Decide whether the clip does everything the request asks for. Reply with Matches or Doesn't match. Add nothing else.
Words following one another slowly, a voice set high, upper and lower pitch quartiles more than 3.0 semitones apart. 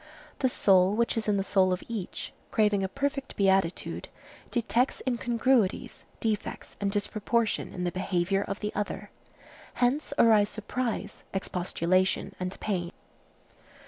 Matches